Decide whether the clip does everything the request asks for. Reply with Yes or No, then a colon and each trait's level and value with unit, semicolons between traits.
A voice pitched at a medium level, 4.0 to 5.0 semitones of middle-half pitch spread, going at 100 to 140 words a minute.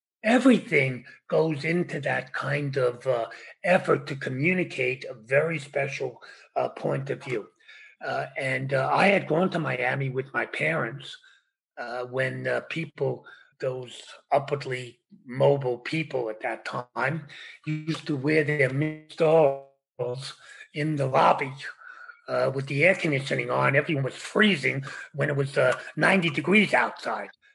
Yes: medium, 145 Hz; average, 4.5 semitones; slow, 135 wpm